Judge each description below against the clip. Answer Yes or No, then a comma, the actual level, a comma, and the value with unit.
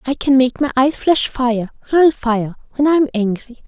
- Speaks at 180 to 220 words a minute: No, average, 165 wpm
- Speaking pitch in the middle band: No, very high, 255 Hz